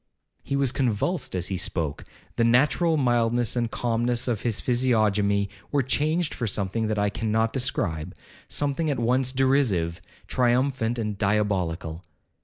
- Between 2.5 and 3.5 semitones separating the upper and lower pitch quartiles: No, average, 4.3 semitones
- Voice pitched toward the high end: No, low, 115 Hz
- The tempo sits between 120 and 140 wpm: Yes, slow, 135 wpm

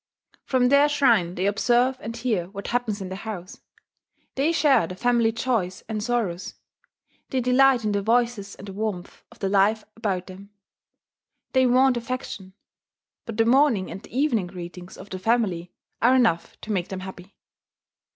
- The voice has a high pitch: Yes, high, 220 Hz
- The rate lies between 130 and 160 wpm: No, average, 170 wpm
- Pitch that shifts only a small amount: No, average, 4.5 semitones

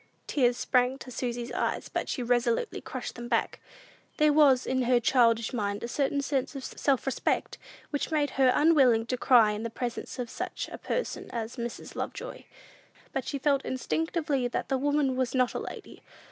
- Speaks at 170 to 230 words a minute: Yes, average, 180 wpm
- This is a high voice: Yes, very high, 255 Hz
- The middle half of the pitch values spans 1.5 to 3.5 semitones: Yes, average, 2.9 semitones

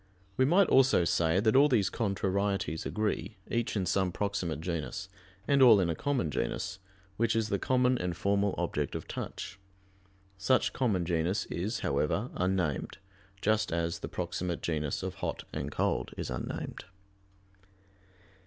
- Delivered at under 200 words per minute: Yes, average, 150 wpm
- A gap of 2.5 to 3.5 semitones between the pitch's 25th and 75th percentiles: No, average, 4.8 semitones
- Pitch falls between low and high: No, low, 100 Hz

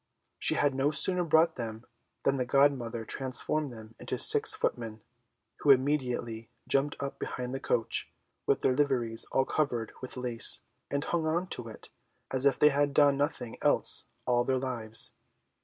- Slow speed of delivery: No, average, 165 wpm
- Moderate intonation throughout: Yes, average, 3.3 semitones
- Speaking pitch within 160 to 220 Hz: No, low, 130 Hz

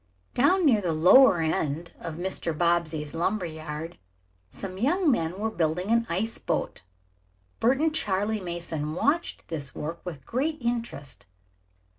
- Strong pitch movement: Yes, wide, 6.4 semitones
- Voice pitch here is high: No, medium, 180 Hz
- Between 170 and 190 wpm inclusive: No, slow, 135 wpm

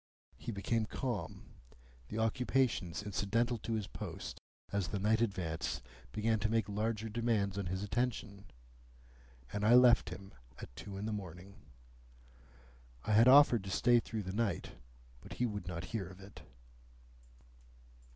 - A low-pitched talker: Yes, low, 105 Hz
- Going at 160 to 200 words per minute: No, average, 150 wpm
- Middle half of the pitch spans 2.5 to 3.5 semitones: Yes, average, 2.9 semitones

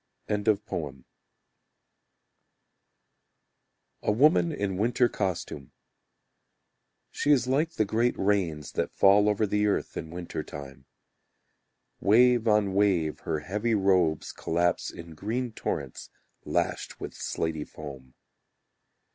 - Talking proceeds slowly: Yes, slow, 105 wpm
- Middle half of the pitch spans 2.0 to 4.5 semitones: No, wide, 5.5 semitones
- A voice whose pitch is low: Yes, low, 100 Hz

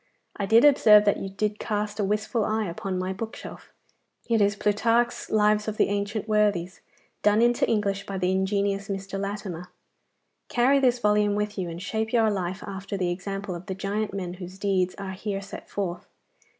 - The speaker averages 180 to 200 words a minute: Yes, average, 185 wpm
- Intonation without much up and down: Yes, narrow, 1.8 semitones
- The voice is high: Yes, high, 205 Hz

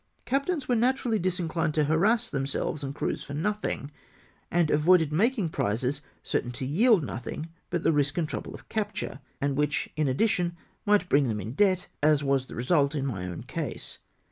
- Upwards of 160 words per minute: Yes, average, 180 wpm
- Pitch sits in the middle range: Yes, medium, 155 Hz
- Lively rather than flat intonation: Yes, wide, 6.2 semitones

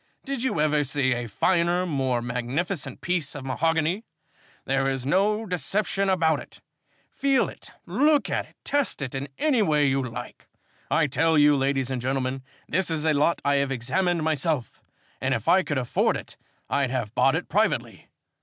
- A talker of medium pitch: Yes, medium, 150 Hz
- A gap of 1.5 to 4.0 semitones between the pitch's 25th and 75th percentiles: No, average, 5.1 semitones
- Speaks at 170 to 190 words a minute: Yes, average, 180 wpm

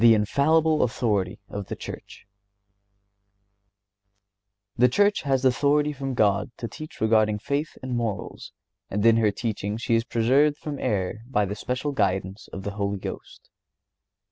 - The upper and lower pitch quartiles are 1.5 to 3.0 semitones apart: No, average, 5.3 semitones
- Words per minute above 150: No, average, 145 wpm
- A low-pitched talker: Yes, low, 115 Hz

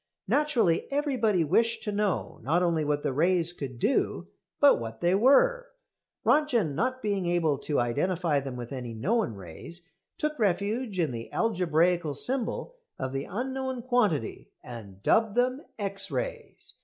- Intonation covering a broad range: Yes, wide, 9.0 semitones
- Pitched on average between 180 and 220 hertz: Yes, medium, 185 Hz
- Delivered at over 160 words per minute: No, average, 150 wpm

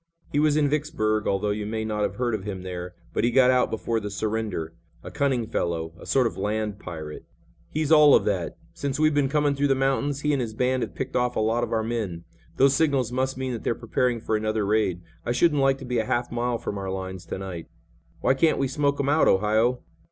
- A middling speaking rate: No, fast, 240 wpm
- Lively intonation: No, average, 4.4 semitones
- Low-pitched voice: Yes, low, 120 Hz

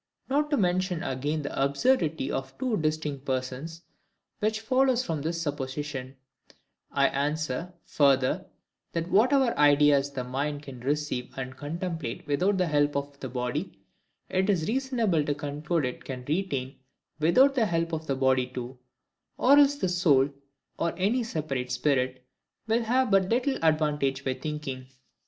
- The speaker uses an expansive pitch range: Yes, wide, 5.7 semitones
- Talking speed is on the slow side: No, average, 145 wpm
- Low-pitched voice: No, medium, 150 Hz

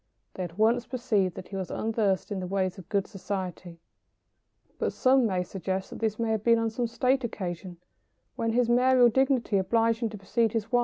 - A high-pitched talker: Yes, high, 220 Hz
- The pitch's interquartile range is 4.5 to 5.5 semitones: No, average, 3.7 semitones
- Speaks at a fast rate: Yes, fast, 210 wpm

